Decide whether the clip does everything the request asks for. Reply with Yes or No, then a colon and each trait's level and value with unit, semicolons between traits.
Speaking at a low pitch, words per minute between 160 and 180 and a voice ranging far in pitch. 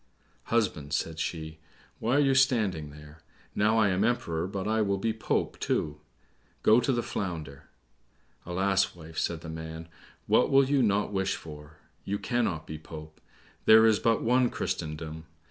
Yes: very low, 95 Hz; average, 165 wpm; wide, 5.8 semitones